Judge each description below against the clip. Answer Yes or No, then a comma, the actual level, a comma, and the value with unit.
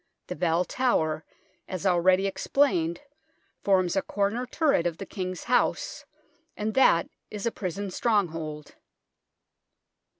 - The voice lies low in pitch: No, medium, 185 Hz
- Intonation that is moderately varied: Yes, average, 3.7 semitones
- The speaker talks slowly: Yes, slow, 120 wpm